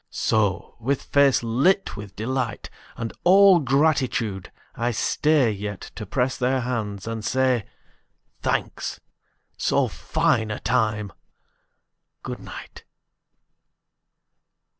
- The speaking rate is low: Yes, slow, 100 wpm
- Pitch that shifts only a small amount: No, average, 4.0 semitones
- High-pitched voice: No, low, 120 Hz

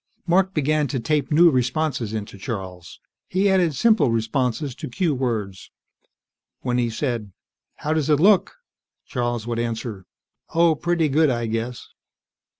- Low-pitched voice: Yes, low, 130 Hz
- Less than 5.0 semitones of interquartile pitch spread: No, wide, 5.5 semitones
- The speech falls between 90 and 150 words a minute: Yes, average, 145 wpm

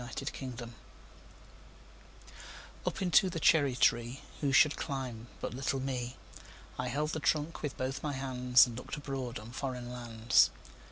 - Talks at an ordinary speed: No, slow, 130 wpm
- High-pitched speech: No, low, 130 Hz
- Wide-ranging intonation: No, average, 2.7 semitones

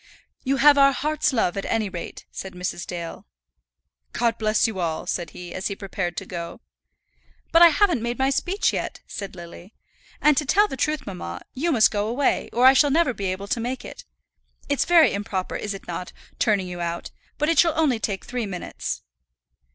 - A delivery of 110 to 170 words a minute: No, average, 200 wpm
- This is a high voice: Yes, high, 225 Hz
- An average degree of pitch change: No, wide, 7.2 semitones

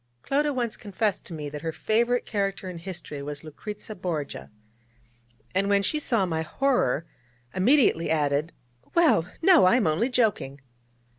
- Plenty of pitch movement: Yes, wide, 6.8 semitones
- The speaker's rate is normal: Yes, average, 150 wpm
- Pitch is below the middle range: No, high, 190 Hz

